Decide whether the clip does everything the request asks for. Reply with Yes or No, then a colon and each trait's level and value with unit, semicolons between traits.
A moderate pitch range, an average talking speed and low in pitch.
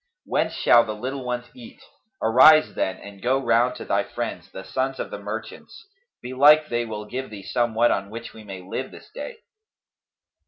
Yes: average, 3.9 semitones; average, 180 wpm; low, 120 Hz